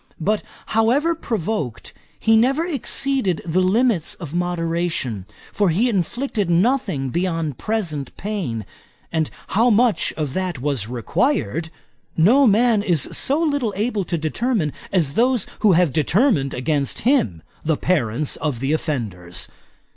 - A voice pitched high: No, medium, 180 Hz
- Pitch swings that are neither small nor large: No, wide, 7.2 semitones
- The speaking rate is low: Yes, slow, 130 wpm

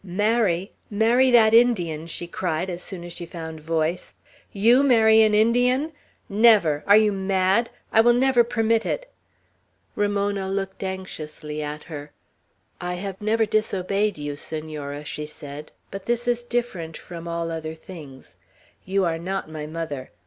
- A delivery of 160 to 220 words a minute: No, average, 150 wpm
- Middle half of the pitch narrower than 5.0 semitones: No, wide, 5.5 semitones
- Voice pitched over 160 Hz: Yes, high, 190 Hz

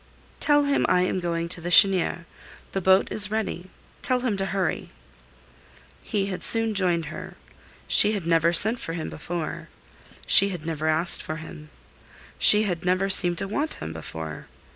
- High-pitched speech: No, medium, 180 Hz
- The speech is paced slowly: No, average, 170 wpm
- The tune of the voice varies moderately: Yes, average, 3.3 semitones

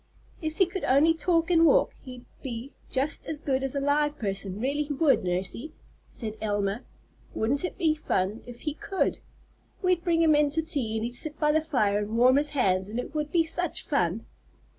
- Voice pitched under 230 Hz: No, very high, 280 Hz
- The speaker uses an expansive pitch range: Yes, wide, 5.7 semitones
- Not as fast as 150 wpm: No, fast, 205 wpm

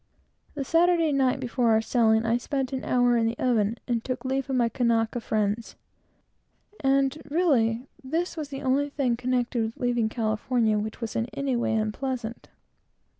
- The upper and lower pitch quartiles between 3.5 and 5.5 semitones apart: No, average, 3.0 semitones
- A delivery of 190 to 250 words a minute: No, average, 170 wpm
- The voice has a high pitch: Yes, high, 245 Hz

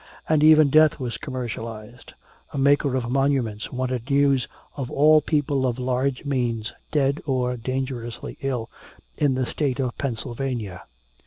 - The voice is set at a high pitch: No, low, 130 Hz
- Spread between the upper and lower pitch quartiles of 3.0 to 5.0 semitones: No, narrow, 2.5 semitones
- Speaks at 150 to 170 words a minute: No, average, 140 wpm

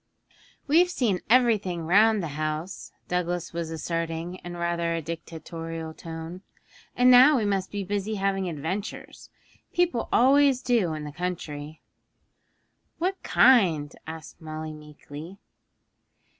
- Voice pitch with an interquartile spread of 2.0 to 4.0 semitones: No, average, 4.9 semitones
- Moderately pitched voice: Yes, medium, 175 Hz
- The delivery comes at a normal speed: No, slow, 120 wpm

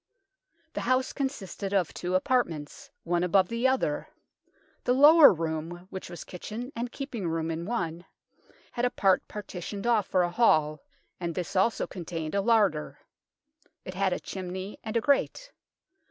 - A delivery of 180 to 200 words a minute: No, average, 155 wpm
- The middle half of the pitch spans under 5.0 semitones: No, wide, 5.5 semitones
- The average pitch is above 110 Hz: Yes, high, 190 Hz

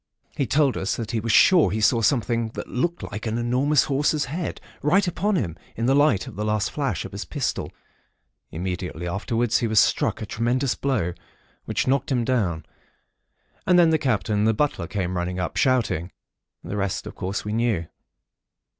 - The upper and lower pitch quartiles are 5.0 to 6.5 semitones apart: Yes, wide, 5.6 semitones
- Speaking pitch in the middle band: No, low, 115 Hz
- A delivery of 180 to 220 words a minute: Yes, average, 190 wpm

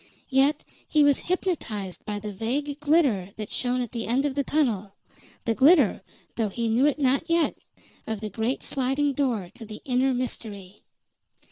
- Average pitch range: Yes, average, 4.9 semitones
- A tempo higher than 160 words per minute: Yes, average, 170 wpm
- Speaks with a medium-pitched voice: No, very high, 250 Hz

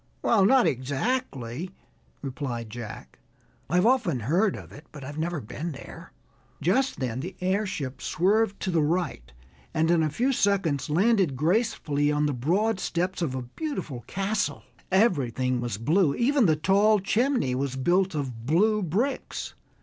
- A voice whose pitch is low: No, medium, 170 Hz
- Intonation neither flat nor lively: No, wide, 6.8 semitones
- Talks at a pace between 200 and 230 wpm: No, average, 150 wpm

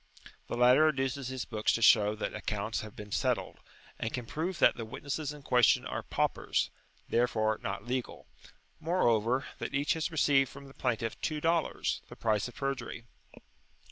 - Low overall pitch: Yes, low, 125 Hz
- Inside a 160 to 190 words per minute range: Yes, average, 170 wpm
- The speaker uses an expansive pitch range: No, average, 4.1 semitones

